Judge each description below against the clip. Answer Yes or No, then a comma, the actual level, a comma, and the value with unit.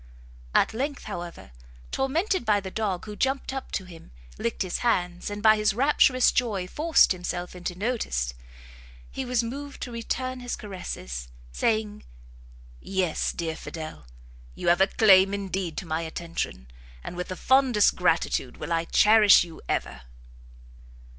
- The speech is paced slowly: No, average, 150 wpm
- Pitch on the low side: No, high, 200 Hz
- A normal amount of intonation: No, wide, 5.7 semitones